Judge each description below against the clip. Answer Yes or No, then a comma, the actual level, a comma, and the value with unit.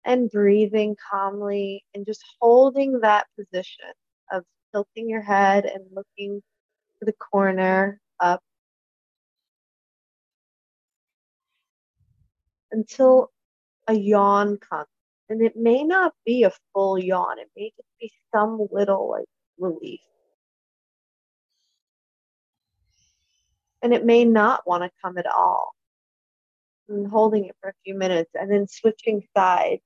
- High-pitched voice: Yes, high, 205 Hz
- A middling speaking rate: No, slow, 115 wpm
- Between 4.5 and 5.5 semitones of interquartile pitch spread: No, average, 2.7 semitones